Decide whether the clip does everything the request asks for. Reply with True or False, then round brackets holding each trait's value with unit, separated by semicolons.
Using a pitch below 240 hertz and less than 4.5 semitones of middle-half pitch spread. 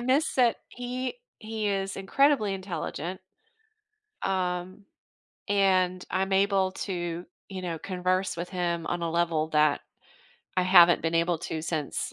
True (185 Hz; 2.4 semitones)